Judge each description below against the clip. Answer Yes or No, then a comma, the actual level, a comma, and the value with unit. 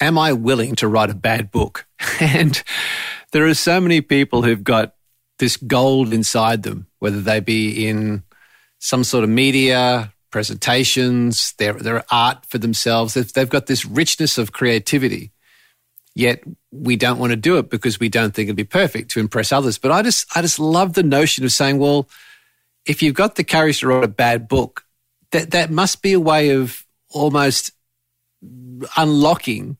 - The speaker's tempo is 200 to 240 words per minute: No, average, 175 wpm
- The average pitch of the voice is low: Yes, low, 125 Hz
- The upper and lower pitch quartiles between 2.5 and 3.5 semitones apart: No, average, 4.5 semitones